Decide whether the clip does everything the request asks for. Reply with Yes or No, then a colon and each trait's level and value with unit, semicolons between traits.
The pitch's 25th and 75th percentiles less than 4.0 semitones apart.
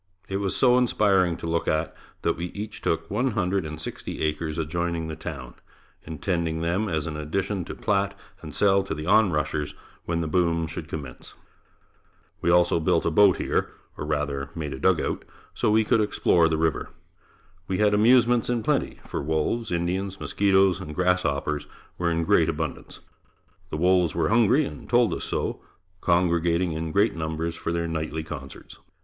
Yes: average, 3.6 semitones